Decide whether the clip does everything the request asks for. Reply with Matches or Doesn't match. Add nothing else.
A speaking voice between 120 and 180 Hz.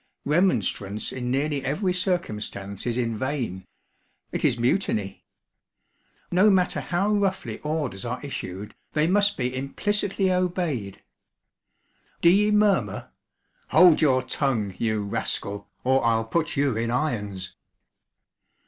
Matches